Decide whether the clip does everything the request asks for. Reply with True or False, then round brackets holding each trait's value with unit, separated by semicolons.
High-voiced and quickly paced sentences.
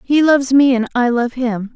True (255 Hz; 240 wpm)